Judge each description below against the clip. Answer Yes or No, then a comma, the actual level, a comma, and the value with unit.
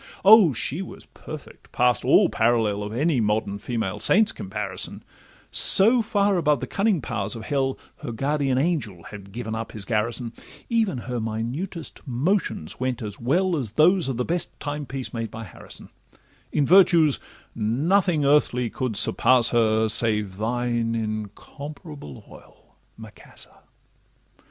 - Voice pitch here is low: Yes, low, 125 Hz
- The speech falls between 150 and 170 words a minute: No, average, 140 wpm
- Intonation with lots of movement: Yes, wide, 5.8 semitones